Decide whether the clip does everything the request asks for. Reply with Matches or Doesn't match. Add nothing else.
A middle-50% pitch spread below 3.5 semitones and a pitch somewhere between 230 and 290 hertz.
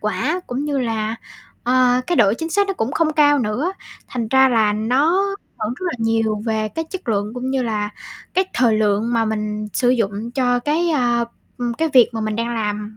Doesn't match